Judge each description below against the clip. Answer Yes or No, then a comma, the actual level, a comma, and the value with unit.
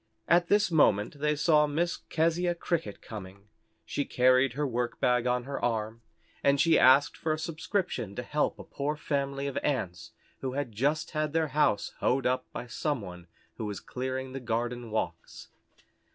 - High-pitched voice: No, low, 135 Hz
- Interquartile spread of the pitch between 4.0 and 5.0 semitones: Yes, average, 4.3 semitones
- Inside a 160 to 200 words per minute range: Yes, average, 170 wpm